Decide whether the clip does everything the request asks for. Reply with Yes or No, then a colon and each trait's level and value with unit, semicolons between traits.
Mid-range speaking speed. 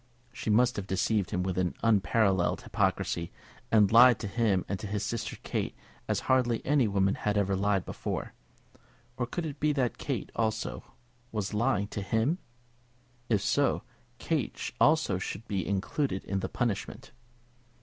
Yes: average, 155 wpm